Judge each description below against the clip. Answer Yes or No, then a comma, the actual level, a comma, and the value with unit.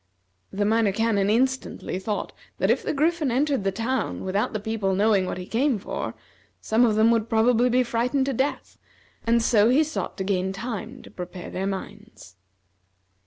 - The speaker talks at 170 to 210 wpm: Yes, average, 180 wpm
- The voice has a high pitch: Yes, high, 225 Hz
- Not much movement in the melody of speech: No, average, 4.1 semitones